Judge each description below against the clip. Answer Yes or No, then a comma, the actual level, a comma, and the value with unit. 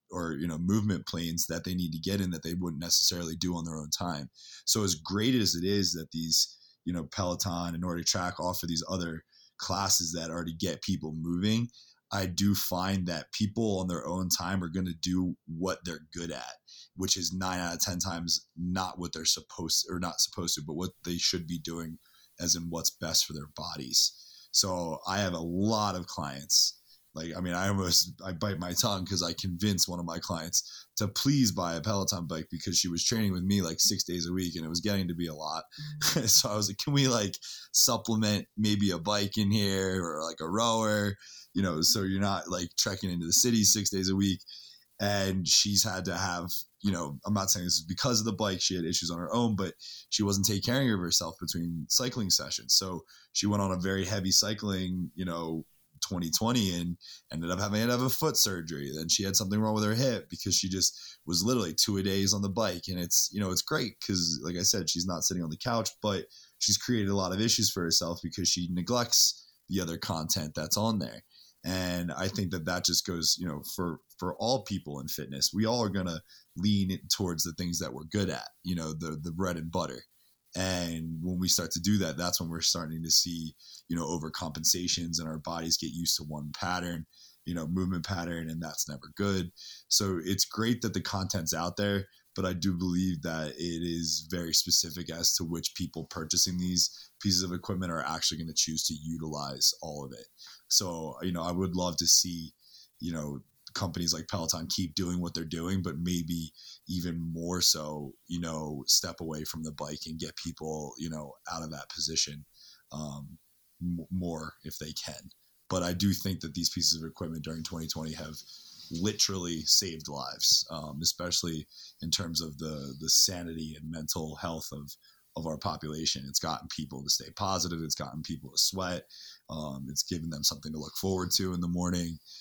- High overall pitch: No, very low, 90 Hz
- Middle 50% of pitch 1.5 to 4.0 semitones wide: Yes, average, 2.9 semitones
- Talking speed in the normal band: No, fast, 215 wpm